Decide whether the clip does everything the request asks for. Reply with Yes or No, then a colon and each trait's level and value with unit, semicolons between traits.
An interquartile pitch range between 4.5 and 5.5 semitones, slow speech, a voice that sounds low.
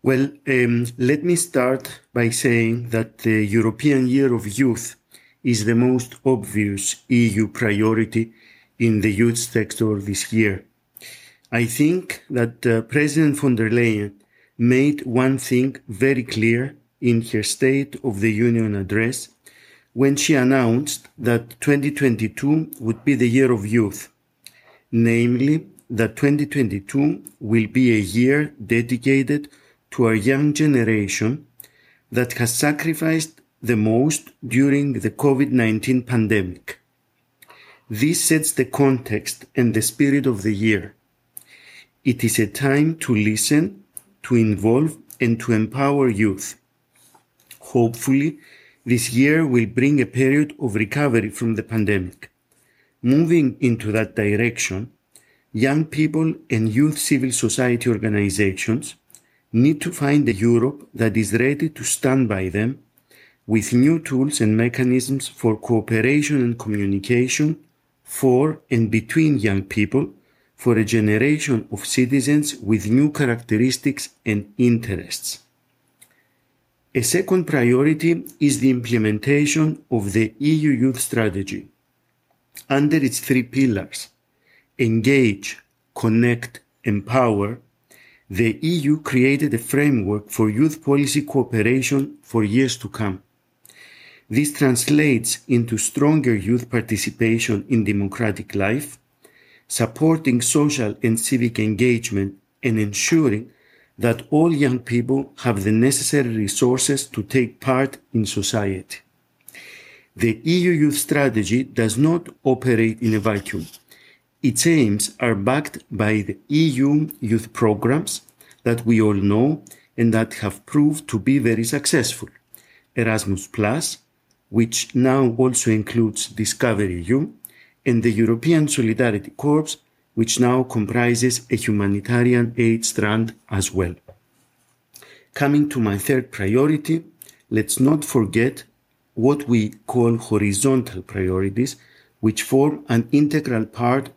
No: average, 3.8 semitones; slow, 120 wpm; low, 120 Hz